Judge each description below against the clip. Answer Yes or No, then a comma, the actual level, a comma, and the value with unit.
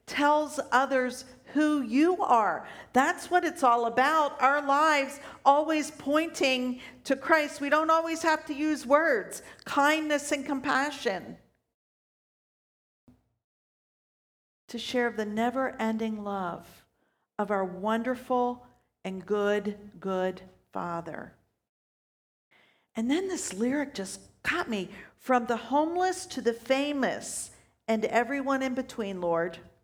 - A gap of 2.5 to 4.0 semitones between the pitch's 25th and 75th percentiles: No, average, 4.8 semitones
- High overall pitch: Yes, very high, 260 Hz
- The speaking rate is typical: No, slow, 115 wpm